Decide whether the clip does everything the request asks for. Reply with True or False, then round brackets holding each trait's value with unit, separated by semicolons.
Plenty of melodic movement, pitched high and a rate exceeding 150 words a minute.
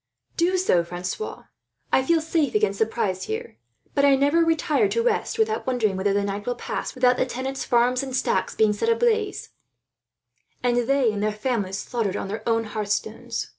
True (7.6 semitones; 250 Hz; 185 wpm)